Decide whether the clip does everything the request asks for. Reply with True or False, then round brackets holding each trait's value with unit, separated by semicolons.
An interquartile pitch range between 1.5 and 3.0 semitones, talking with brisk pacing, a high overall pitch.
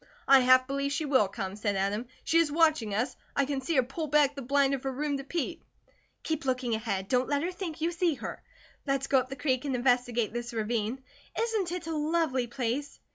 False (3.8 semitones; 225 wpm; 270 Hz)